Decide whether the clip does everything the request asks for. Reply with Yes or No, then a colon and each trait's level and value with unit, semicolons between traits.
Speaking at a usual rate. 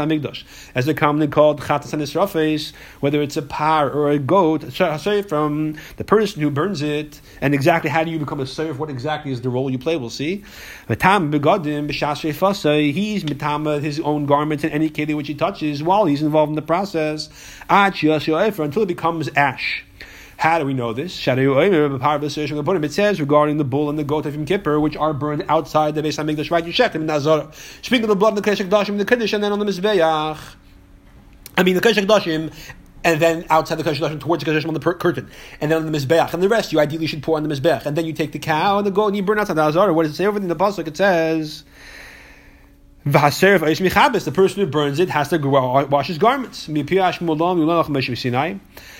Yes: average, 195 wpm